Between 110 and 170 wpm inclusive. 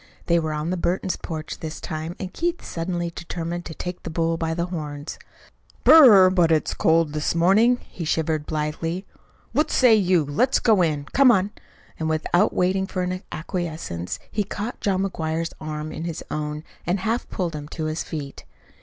No: average, 180 wpm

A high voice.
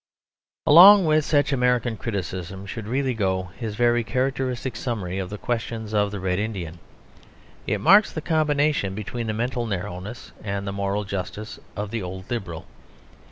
No: low, 110 Hz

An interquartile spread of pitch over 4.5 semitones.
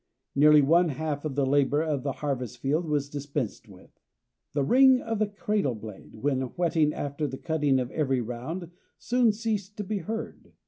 Yes: average, 5.1 semitones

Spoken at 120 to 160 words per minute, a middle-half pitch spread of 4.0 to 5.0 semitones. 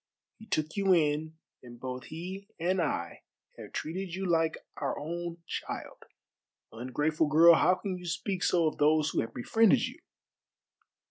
No: average, 155 wpm; average, 3.4 semitones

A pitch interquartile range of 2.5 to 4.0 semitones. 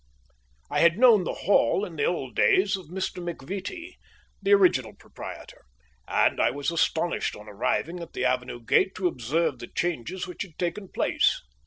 No: average, 5.2 semitones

